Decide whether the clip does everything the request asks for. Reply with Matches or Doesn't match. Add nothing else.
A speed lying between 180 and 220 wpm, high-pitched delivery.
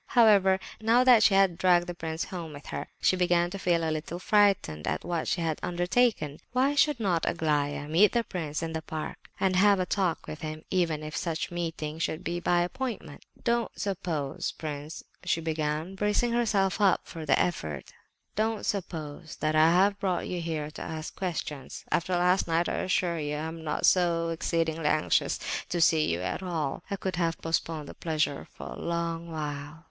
Doesn't match